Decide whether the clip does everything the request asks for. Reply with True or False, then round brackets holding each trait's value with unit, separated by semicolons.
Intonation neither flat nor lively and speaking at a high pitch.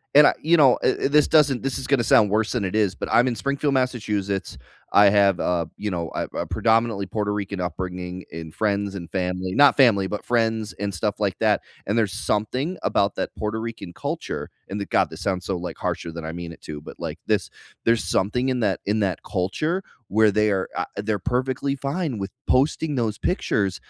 False (4.7 semitones; 105 Hz)